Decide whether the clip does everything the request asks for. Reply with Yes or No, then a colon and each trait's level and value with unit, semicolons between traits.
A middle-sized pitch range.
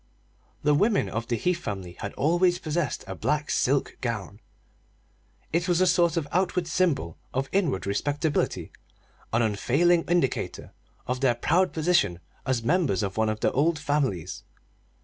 No: wide, 7.1 semitones